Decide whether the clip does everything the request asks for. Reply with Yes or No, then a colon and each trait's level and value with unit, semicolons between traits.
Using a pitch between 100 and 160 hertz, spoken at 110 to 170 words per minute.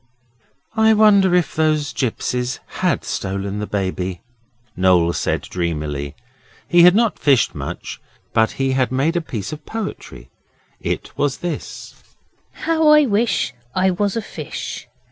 Yes: medium, 140 Hz; average, 140 wpm